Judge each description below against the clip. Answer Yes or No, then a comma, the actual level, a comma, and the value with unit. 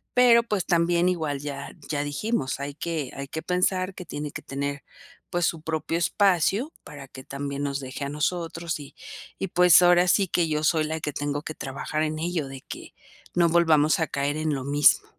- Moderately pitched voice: Yes, medium, 155 Hz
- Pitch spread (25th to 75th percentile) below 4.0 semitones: Yes, average, 3.6 semitones